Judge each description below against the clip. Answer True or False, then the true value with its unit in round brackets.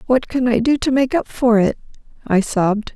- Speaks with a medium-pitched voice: False (240 Hz)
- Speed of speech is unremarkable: False (225 wpm)